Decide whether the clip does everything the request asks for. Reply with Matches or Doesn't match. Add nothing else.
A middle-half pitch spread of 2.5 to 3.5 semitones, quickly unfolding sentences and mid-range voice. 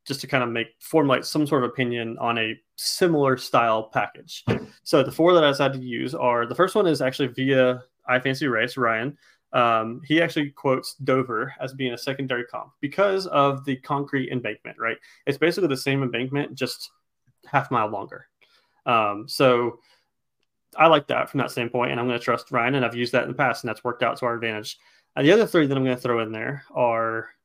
Doesn't match